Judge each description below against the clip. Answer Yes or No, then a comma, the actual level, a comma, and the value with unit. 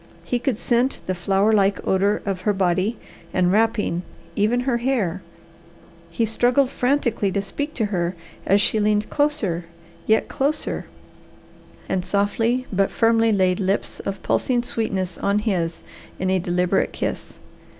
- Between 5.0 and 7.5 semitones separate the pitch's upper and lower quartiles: No, average, 3.9 semitones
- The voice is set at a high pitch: Yes, high, 205 Hz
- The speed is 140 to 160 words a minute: Yes, average, 145 wpm